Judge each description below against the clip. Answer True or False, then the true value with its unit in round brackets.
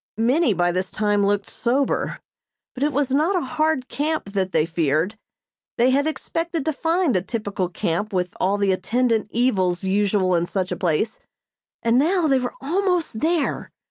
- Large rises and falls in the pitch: True (7.5 semitones)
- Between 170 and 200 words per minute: True (175 wpm)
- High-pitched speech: True (225 Hz)